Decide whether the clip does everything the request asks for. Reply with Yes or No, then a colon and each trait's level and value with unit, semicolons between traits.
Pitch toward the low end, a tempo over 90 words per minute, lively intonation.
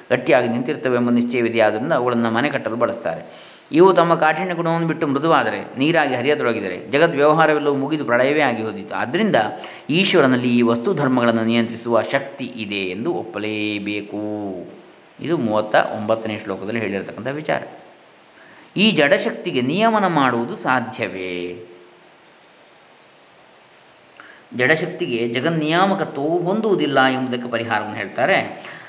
Yes: low, 120 Hz; fast, 105 wpm; wide, 6.3 semitones